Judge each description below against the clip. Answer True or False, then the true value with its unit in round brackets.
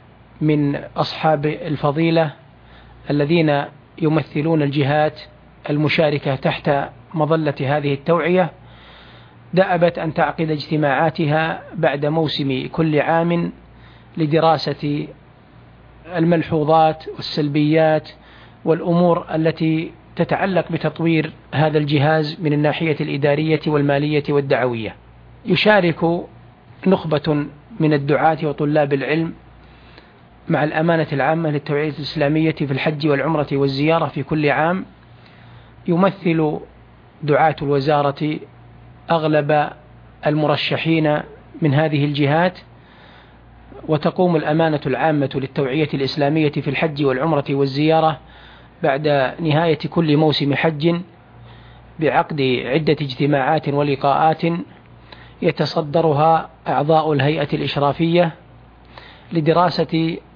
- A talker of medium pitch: True (155 Hz)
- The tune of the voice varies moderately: False (2.2 semitones)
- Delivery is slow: False (80 wpm)